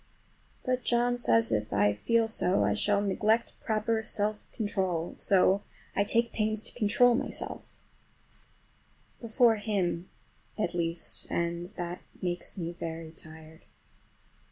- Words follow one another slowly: Yes, slow, 115 wpm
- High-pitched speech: Yes, high, 200 Hz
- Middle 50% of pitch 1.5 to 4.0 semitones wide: No, average, 4.6 semitones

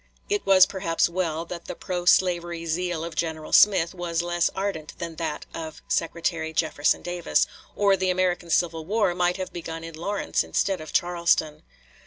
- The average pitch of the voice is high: No, medium, 175 Hz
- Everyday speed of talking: Yes, average, 170 wpm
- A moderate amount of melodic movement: No, narrow, 2.0 semitones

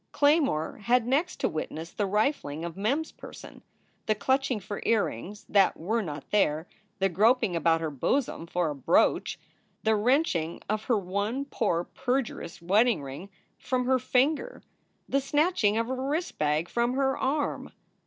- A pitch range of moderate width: No, wide, 7.4 semitones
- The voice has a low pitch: No, high, 215 Hz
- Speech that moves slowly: No, average, 160 wpm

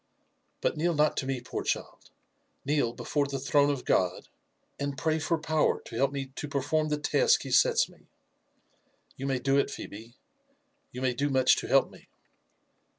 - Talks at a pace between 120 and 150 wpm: No, average, 185 wpm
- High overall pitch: No, medium, 140 Hz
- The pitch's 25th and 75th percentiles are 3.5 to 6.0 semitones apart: No, average, 2.9 semitones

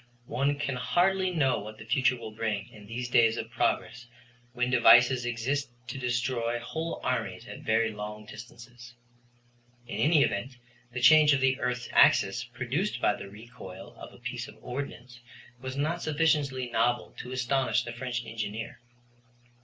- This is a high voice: No, low, 125 Hz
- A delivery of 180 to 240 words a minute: No, average, 160 wpm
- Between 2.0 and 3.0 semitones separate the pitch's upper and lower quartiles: Yes, average, 2.7 semitones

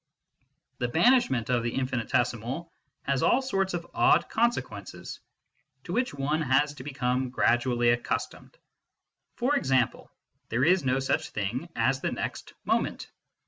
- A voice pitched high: No, low, 135 Hz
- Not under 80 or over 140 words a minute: Yes, slow, 135 wpm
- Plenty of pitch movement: Yes, wide, 6.1 semitones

